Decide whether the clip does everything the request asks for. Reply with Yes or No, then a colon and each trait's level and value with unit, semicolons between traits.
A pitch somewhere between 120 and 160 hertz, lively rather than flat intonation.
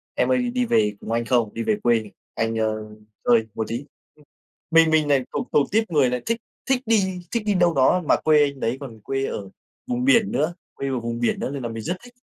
Yes: medium, 140 Hz; wide, 8.3 semitones